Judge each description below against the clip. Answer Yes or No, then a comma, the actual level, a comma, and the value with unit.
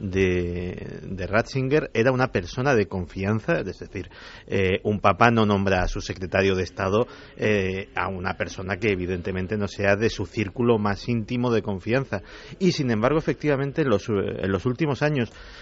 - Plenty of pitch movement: No, average, 3.8 semitones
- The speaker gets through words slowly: No, average, 175 wpm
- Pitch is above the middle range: No, low, 105 Hz